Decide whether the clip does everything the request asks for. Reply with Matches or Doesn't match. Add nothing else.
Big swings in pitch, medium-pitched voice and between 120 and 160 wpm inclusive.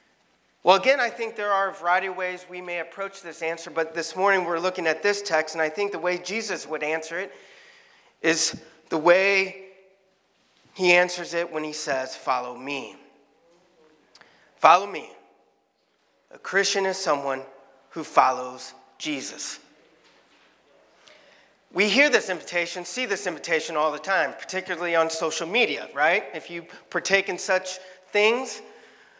Doesn't match